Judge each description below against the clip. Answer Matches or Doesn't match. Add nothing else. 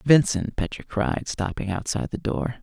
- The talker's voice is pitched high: Doesn't match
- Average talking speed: Matches